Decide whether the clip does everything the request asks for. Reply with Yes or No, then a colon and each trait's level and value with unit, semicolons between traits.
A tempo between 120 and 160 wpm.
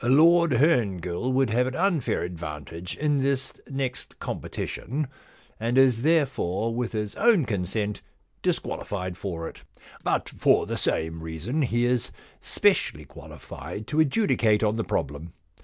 Yes: average, 140 wpm